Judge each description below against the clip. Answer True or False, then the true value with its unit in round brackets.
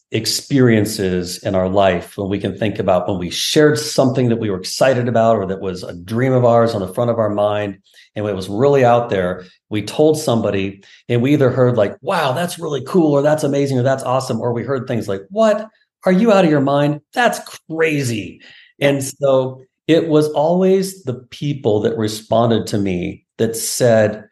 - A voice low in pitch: True (120 Hz)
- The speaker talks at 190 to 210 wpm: True (200 wpm)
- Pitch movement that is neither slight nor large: False (5.7 semitones)